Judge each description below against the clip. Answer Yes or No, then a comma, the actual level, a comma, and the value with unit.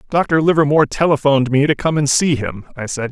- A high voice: No, medium, 140 Hz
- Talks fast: Yes, fast, 210 wpm